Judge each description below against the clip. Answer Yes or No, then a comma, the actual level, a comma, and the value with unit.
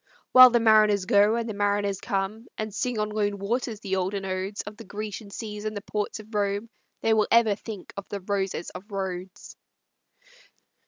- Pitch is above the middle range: Yes, high, 205 Hz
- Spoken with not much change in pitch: Yes, narrow, 1.6 semitones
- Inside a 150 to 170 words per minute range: No, average, 190 wpm